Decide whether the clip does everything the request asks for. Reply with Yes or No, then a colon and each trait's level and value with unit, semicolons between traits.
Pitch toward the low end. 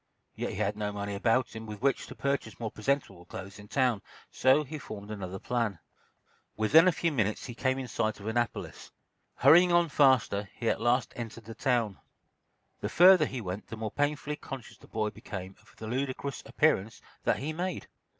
Yes: low, 115 Hz